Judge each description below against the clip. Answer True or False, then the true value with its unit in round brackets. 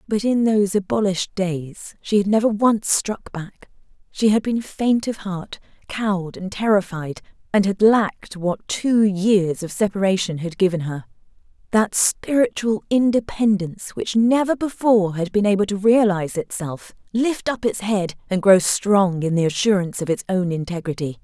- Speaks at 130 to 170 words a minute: True (160 wpm)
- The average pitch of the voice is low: False (200 Hz)